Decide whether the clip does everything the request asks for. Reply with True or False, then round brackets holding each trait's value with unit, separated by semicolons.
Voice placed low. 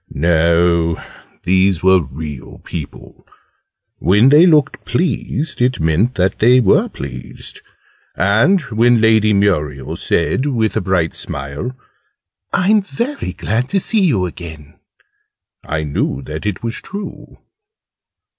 True (100 Hz)